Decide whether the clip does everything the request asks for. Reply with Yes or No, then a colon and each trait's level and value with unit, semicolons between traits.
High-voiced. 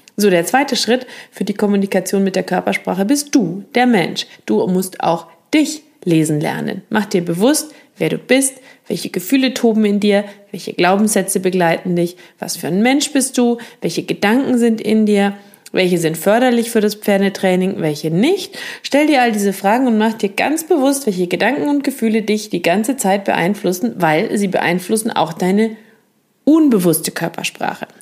Yes: high, 210 Hz